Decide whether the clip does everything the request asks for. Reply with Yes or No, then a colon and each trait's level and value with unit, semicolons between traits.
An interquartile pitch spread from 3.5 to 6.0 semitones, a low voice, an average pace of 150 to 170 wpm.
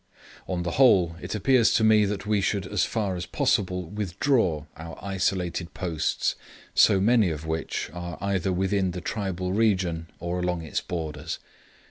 No: average, 3.0 semitones; very low, 95 Hz; average, 160 wpm